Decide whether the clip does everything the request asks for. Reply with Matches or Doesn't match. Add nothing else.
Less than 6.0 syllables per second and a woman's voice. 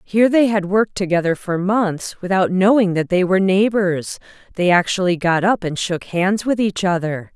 Matches